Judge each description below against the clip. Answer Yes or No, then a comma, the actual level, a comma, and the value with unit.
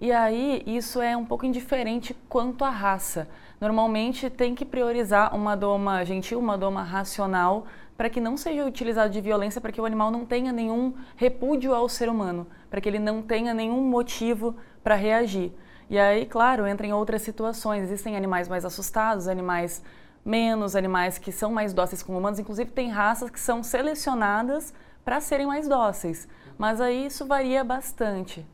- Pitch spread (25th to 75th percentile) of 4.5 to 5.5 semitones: No, average, 3.4 semitones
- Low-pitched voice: No, high, 225 Hz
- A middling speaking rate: Yes, average, 170 wpm